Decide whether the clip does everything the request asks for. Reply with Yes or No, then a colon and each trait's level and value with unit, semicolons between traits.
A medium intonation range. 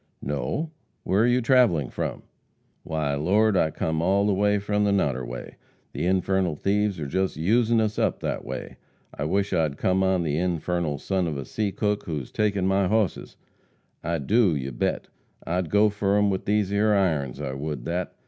Yes: average, 4.9 semitones